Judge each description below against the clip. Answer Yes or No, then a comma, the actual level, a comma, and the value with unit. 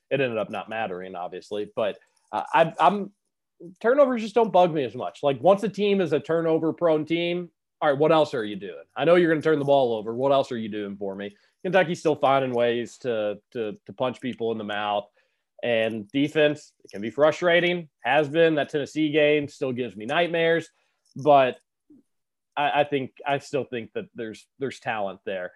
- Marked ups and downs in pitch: Yes, wide, 6.3 semitones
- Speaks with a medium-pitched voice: Yes, medium, 150 Hz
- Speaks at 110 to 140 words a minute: No, fast, 205 wpm